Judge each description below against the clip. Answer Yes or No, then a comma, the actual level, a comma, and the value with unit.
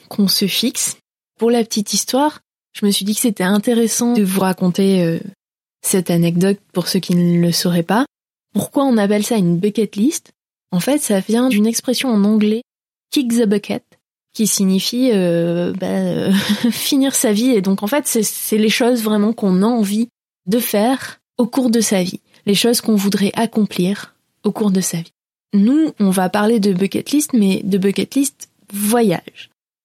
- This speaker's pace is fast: No, average, 190 wpm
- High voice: Yes, high, 210 Hz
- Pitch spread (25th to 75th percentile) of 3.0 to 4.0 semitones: Yes, average, 3.5 semitones